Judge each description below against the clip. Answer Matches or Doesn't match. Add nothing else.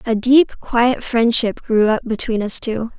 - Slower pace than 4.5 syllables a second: Matches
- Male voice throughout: Doesn't match